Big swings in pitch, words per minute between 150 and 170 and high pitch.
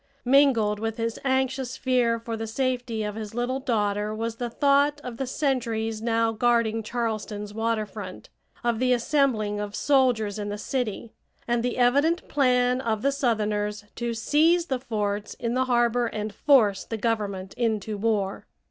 No: average, 3.0 semitones; average, 165 wpm; high, 230 Hz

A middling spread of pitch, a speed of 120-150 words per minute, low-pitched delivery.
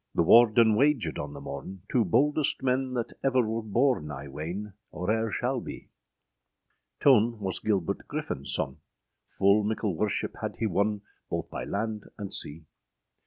No: average, 4.3 semitones; average, 165 wpm; low, 105 Hz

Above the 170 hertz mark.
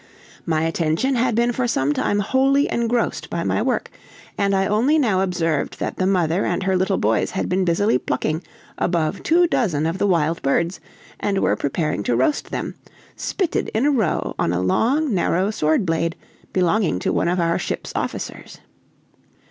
Yes: medium, 185 Hz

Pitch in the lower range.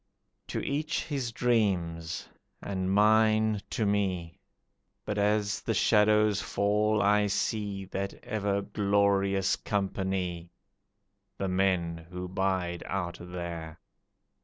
Yes: low, 100 Hz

